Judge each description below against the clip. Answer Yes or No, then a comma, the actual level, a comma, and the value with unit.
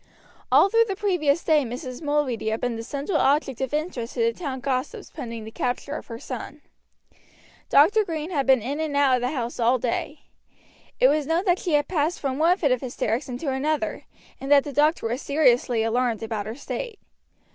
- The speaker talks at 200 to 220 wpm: Yes, fast, 205 wpm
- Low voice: No, very high, 280 Hz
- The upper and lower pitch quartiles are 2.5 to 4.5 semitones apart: Yes, average, 4.2 semitones